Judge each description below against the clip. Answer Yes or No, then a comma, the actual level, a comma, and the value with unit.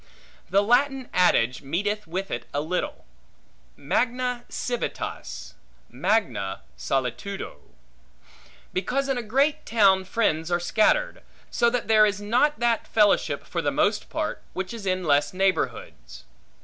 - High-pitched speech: Yes, high, 205 Hz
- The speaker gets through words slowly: Yes, slow, 130 wpm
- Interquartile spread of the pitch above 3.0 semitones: Yes, wide, 5.4 semitones